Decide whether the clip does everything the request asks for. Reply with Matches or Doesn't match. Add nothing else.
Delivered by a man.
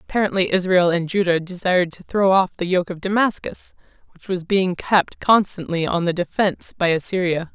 Doesn't match